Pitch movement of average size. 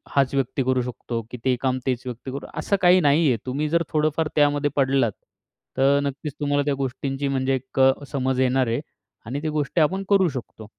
No: narrow, 2.2 semitones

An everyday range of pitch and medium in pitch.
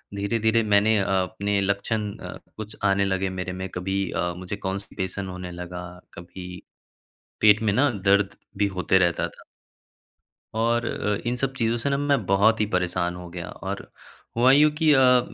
No: average, 3.5 semitones; low, 100 Hz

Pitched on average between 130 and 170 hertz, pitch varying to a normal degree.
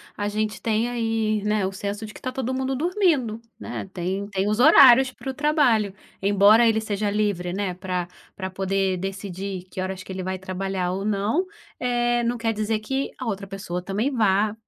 No: high, 210 Hz; average, 3.6 semitones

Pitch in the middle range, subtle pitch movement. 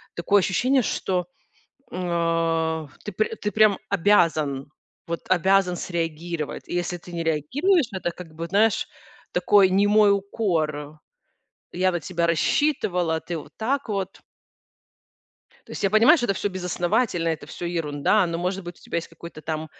No: medium, 180 Hz; average, 3.6 semitones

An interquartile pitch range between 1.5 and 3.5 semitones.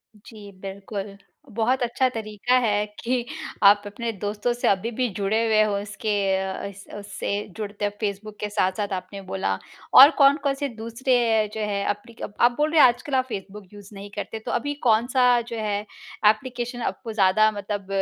Yes: average, 3.0 semitones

